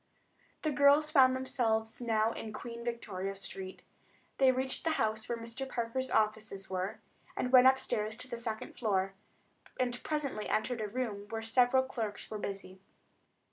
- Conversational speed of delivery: Yes, average, 150 wpm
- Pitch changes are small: No, average, 3.3 semitones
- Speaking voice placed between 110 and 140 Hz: No, high, 230 Hz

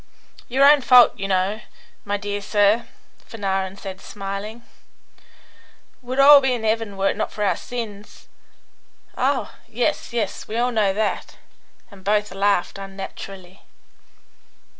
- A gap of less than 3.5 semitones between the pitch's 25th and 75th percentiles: Yes, average, 3.0 semitones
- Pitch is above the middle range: Yes, high, 205 Hz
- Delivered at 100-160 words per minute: Yes, average, 140 wpm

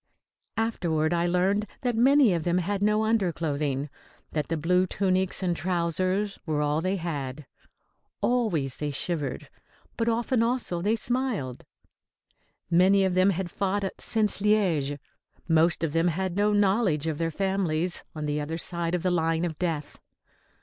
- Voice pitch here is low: No, medium, 180 Hz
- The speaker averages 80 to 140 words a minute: No, average, 155 wpm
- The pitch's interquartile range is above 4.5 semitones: No, average, 4.1 semitones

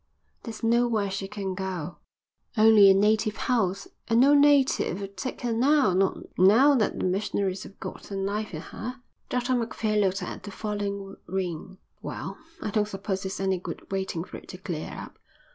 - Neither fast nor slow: Yes, average, 180 wpm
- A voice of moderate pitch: No, high, 200 Hz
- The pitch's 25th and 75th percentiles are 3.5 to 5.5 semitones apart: No, average, 3.0 semitones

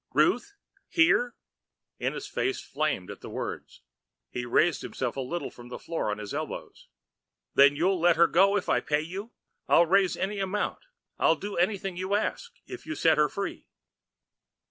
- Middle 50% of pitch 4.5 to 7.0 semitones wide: Yes, average, 5.0 semitones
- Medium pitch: Yes, medium, 175 Hz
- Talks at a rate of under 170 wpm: No, average, 175 wpm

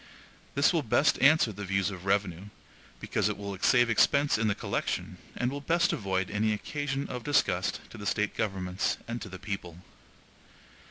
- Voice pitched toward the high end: No, low, 105 Hz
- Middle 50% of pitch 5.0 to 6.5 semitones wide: Yes, average, 5.3 semitones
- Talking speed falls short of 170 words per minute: No, average, 175 wpm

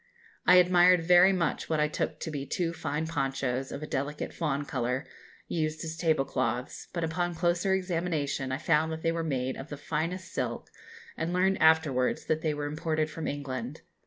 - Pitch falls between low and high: Yes, medium, 155 Hz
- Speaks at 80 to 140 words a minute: No, average, 190 wpm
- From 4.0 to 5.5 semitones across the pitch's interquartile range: No, average, 3.1 semitones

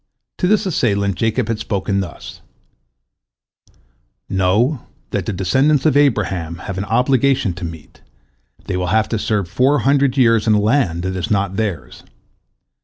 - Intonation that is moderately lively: No, wide, 5.7 semitones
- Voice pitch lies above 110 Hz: No, low, 105 Hz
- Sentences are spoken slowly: No, average, 155 wpm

